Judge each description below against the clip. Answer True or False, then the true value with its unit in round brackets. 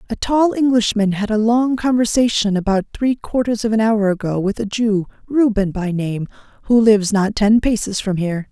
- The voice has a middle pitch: False (215 Hz)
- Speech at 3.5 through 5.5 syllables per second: True (5.1 syllables/s)